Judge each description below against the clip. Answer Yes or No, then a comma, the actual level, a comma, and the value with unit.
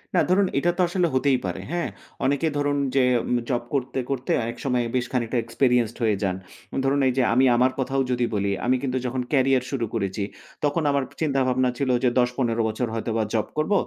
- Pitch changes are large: No, average, 2.7 semitones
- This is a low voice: Yes, low, 130 Hz